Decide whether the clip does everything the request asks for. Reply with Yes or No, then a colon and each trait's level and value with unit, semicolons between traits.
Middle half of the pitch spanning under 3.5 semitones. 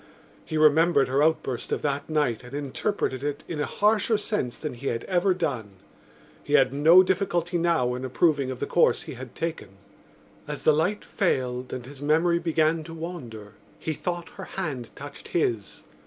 No: average, 4.8 semitones